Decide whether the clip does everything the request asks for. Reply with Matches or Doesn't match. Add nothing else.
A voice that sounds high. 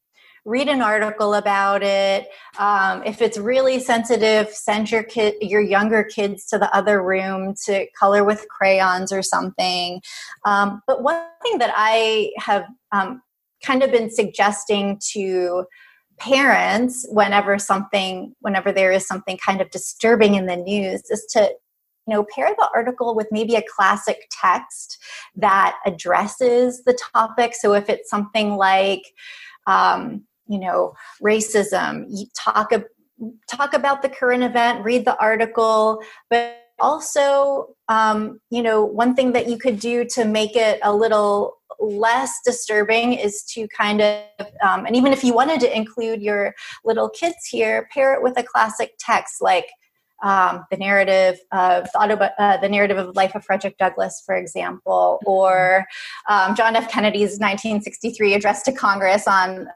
Matches